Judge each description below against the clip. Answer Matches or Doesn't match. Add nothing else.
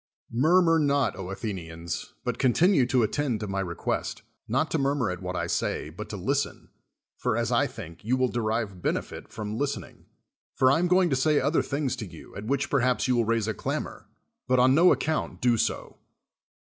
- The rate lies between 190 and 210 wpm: Matches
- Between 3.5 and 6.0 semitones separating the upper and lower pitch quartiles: Matches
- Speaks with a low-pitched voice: Matches